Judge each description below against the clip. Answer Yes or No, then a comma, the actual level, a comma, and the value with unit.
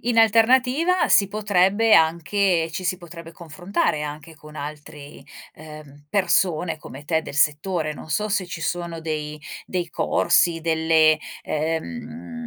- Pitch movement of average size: Yes, average, 4.2 semitones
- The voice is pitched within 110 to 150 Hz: No, medium, 165 Hz